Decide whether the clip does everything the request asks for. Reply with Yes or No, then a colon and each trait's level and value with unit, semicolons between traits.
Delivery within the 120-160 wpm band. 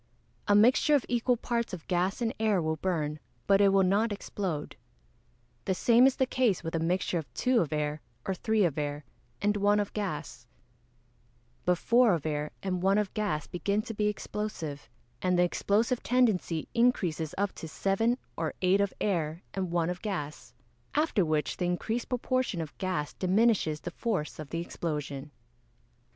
No: average, 175 wpm